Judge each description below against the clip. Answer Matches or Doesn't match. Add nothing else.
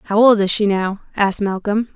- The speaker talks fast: Matches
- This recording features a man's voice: Doesn't match